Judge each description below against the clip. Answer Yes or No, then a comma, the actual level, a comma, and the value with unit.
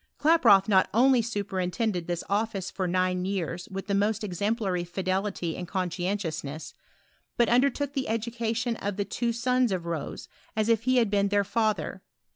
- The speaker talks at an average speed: Yes, average, 160 wpm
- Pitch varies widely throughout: No, average, 3.8 semitones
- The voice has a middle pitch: No, high, 200 Hz